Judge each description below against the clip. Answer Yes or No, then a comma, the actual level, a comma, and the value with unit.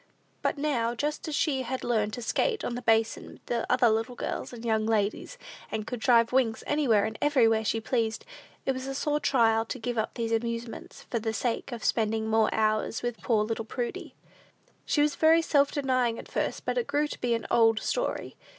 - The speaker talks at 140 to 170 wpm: No, fast, 205 wpm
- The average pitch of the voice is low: No, high, 235 Hz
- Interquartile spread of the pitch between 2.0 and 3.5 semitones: Yes, average, 2.9 semitones